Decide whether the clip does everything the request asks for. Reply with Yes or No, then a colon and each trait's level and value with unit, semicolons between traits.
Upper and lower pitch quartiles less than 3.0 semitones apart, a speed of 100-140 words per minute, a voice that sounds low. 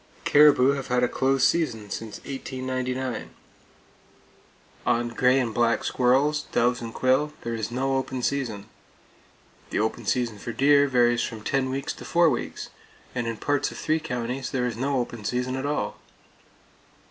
No: narrow, 2.4 semitones; average, 160 wpm; low, 125 Hz